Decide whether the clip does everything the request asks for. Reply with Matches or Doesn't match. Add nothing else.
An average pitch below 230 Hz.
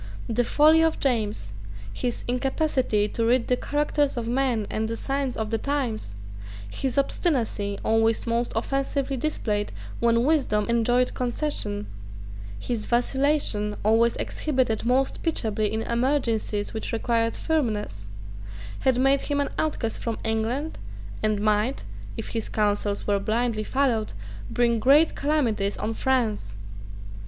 Doesn't match